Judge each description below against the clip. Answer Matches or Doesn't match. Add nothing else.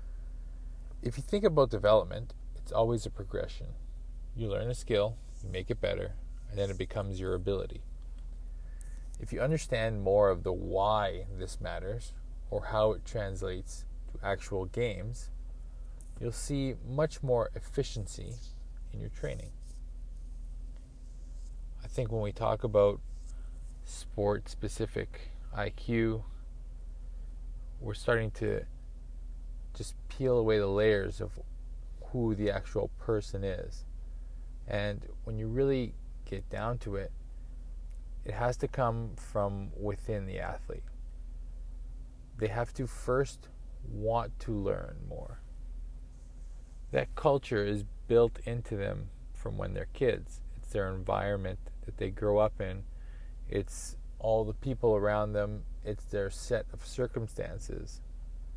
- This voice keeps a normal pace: Doesn't match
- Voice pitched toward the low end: Matches